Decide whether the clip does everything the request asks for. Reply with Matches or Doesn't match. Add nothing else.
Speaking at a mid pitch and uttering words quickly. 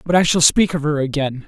Matches